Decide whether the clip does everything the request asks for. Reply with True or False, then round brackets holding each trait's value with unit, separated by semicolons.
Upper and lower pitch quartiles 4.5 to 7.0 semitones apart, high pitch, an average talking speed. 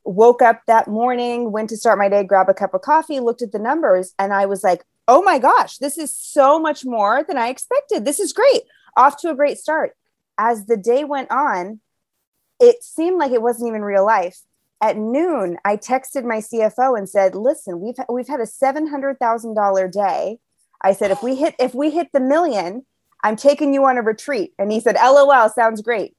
False (4.9 semitones; 240 Hz; 210 wpm)